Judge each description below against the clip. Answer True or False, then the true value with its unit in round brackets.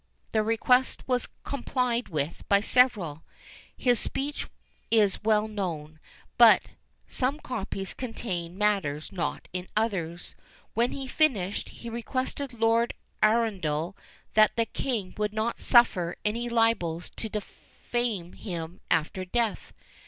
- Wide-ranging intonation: False (4.8 semitones)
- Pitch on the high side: True (215 Hz)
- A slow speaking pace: True (120 wpm)